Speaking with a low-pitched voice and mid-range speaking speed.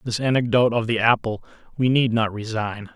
Yes: low, 115 Hz; average, 185 wpm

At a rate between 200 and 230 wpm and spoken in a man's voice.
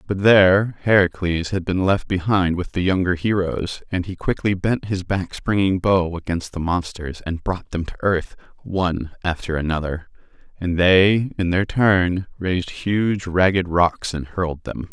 No: average, 170 wpm; male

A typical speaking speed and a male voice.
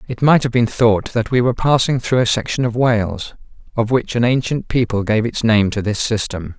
No: fast, 230 wpm; male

